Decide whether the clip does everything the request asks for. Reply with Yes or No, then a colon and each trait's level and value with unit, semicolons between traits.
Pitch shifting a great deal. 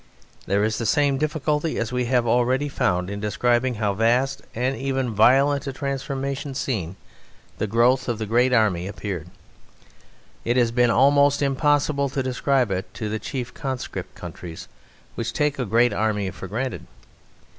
No: average, 3.8 semitones